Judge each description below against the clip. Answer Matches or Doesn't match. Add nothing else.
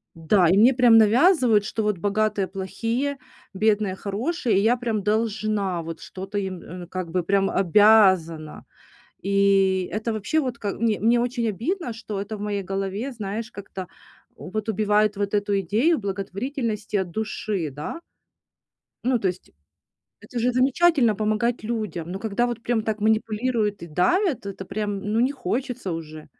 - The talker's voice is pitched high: Matches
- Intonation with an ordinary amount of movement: Matches